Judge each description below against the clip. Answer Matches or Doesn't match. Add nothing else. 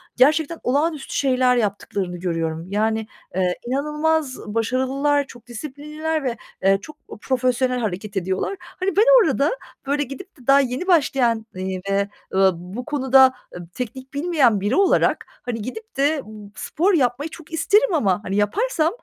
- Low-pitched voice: Doesn't match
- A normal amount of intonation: Doesn't match